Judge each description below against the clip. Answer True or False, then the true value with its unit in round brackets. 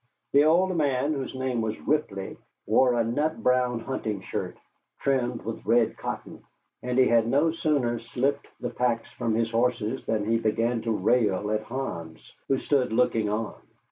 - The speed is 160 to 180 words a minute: True (170 wpm)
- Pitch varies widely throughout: False (3.1 semitones)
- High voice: False (120 Hz)